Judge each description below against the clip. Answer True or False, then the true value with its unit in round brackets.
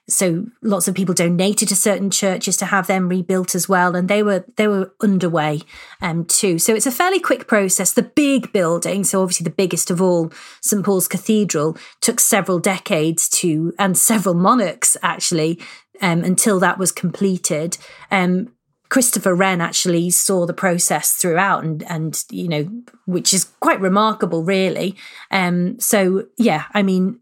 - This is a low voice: False (190 Hz)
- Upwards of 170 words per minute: False (165 wpm)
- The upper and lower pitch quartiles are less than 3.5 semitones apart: True (2.8 semitones)